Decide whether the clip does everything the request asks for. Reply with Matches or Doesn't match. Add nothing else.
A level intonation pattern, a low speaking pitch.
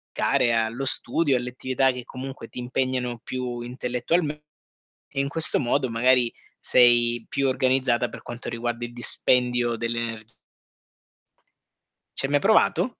Matches